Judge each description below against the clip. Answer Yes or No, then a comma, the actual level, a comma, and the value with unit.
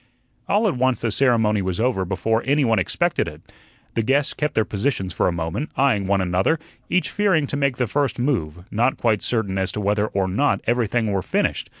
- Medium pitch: No, low, 115 Hz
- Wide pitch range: Yes, wide, 5.7 semitones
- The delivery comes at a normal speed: No, fast, 210 wpm